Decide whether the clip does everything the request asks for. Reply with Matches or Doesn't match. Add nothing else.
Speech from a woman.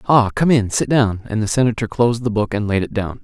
Doesn't match